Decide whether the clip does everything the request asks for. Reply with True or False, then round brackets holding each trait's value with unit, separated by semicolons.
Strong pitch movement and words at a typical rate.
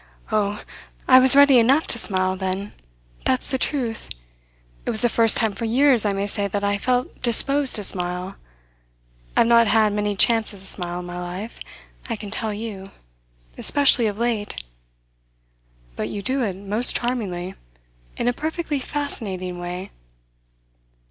False (4.0 semitones; 155 wpm)